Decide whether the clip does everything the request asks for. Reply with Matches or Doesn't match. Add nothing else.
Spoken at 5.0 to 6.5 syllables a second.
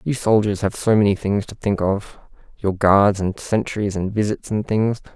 Doesn't match